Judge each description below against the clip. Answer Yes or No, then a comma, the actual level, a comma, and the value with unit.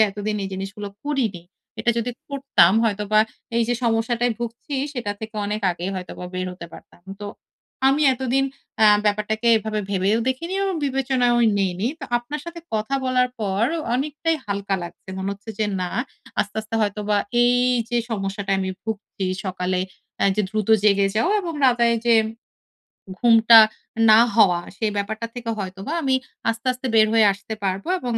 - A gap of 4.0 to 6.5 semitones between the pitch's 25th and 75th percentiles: No, average, 3.6 semitones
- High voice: Yes, high, 220 Hz